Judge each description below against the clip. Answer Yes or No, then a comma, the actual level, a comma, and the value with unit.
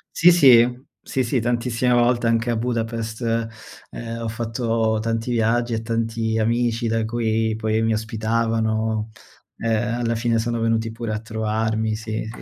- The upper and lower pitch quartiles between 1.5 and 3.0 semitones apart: No, narrow, 1.0 semitones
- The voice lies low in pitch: Yes, low, 115 Hz